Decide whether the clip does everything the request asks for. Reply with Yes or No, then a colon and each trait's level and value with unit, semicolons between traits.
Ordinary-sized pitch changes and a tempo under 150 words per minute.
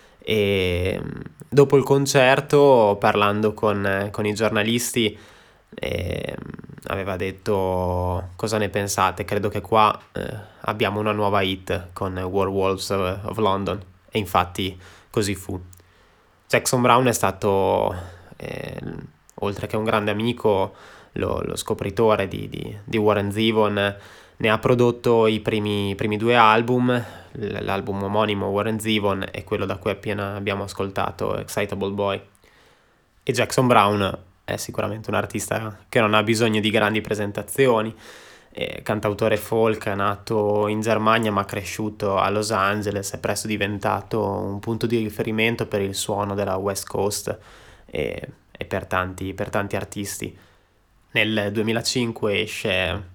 No: narrow, 1.9 semitones; average, 135 wpm